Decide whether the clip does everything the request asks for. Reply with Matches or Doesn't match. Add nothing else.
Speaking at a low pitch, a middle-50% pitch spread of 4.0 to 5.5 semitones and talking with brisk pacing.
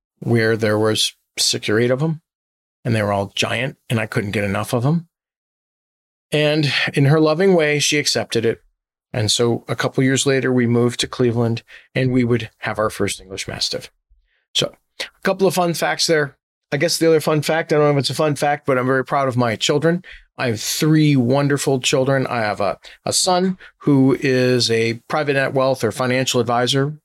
Matches